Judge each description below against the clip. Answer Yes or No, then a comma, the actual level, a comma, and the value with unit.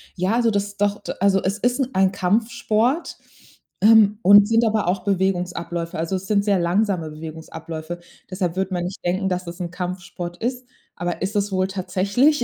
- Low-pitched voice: No, high, 190 Hz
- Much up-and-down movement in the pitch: No, average, 2.9 semitones